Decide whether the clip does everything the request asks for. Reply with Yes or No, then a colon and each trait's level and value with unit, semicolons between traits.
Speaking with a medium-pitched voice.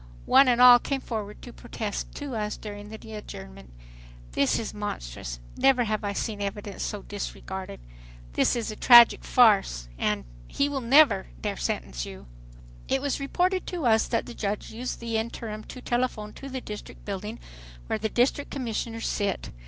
No: high, 220 Hz